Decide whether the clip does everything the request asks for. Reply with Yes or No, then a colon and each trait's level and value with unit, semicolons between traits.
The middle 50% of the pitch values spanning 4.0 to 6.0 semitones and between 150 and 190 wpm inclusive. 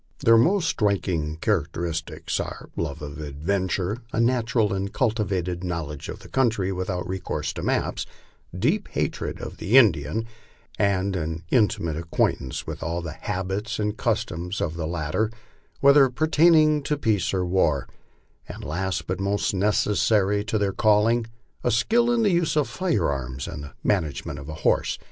Yes: wide, 5.6 semitones; average, 160 wpm